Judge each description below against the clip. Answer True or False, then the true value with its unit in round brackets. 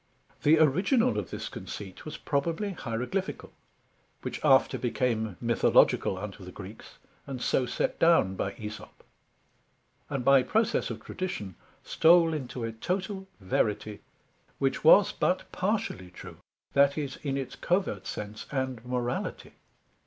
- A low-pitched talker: True (130 Hz)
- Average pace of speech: False (130 wpm)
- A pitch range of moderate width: False (7.2 semitones)